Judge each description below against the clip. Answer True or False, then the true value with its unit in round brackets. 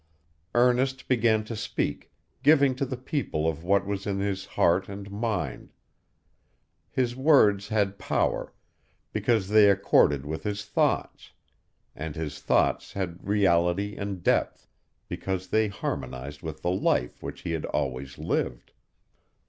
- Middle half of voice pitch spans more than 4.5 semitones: True (5.1 semitones)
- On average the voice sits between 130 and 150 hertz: False (100 Hz)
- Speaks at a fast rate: False (135 wpm)